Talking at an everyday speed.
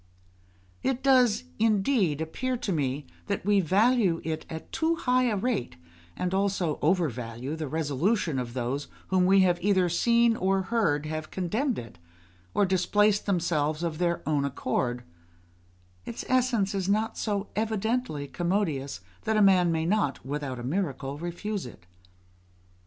Yes: average, 150 wpm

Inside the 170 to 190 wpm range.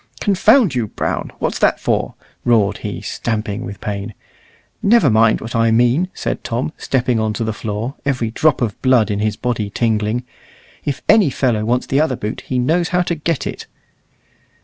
Yes: average, 180 wpm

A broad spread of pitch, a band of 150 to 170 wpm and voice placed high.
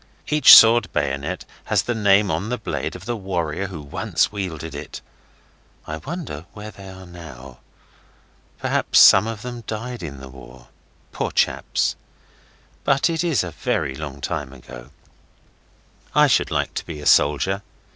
No: wide, 7.2 semitones; average, 155 wpm; very low, 90 Hz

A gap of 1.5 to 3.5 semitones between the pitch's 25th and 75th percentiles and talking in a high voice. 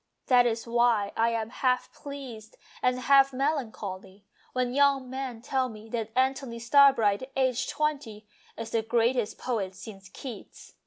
Yes: average, 3.1 semitones; high, 240 Hz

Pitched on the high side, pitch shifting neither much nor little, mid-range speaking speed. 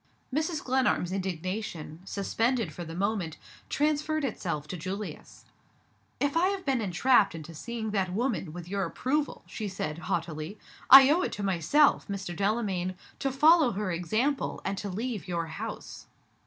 No: high, 200 Hz; wide, 6.9 semitones; average, 155 wpm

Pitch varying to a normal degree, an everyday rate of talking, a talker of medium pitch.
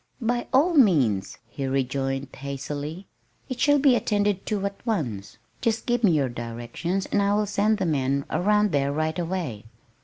No: wide, 7.6 semitones; average, 165 wpm; medium, 175 Hz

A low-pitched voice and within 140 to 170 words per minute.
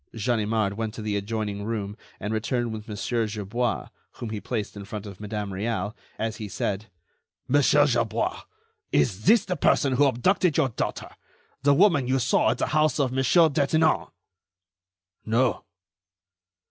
Yes: low, 115 Hz; average, 155 wpm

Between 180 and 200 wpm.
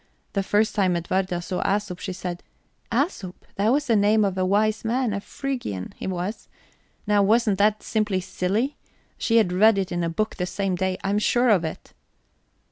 Yes: average, 190 wpm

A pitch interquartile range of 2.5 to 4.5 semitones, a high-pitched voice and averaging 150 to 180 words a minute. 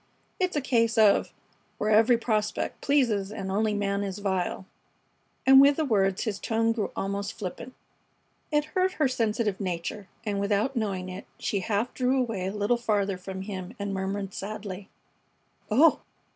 Yes: average, 3.2 semitones; high, 210 Hz; average, 160 wpm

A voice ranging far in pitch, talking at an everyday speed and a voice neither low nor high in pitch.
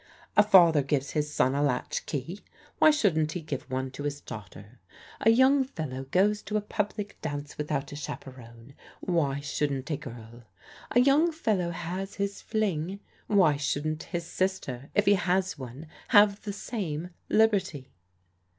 Yes: wide, 6.3 semitones; average, 160 wpm; medium, 160 Hz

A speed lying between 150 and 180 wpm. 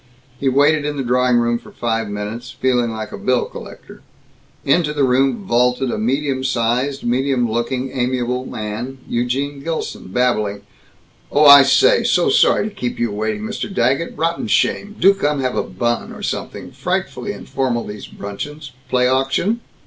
Yes: average, 165 wpm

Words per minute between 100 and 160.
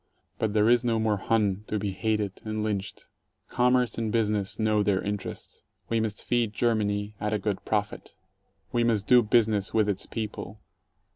No: average, 185 wpm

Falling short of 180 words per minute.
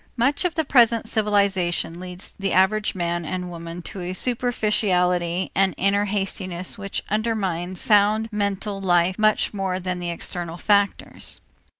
Yes: average, 140 wpm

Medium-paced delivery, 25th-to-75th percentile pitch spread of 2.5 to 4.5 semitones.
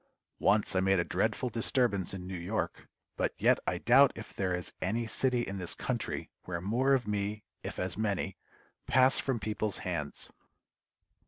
Yes: average, 170 wpm; average, 4.2 semitones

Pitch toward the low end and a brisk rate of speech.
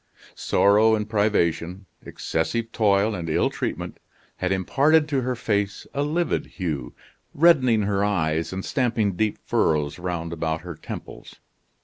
No: low, 100 Hz; slow, 135 wpm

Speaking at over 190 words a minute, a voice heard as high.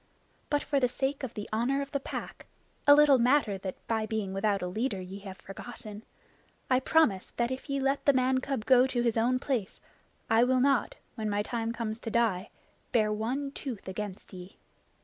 Yes: average, 200 wpm; high, 235 Hz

